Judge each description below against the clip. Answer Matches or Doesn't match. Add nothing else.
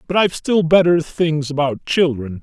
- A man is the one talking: Matches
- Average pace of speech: Matches